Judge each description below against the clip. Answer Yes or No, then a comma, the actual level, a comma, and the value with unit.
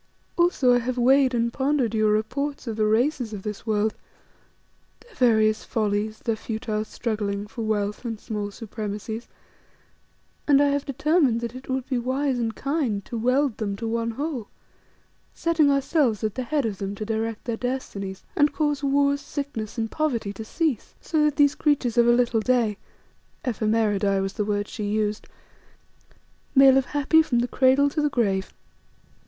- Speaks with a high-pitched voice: Yes, high, 235 Hz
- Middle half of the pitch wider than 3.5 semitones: Yes, average, 4.4 semitones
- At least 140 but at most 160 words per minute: No, average, 170 wpm